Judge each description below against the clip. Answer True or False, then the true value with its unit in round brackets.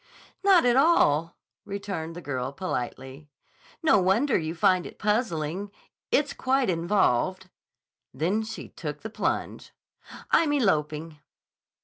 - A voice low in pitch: False (185 Hz)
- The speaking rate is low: True (115 wpm)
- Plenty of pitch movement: True (6.0 semitones)